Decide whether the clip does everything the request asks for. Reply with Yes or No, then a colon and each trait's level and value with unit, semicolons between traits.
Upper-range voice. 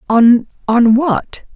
Yes: high, 235 Hz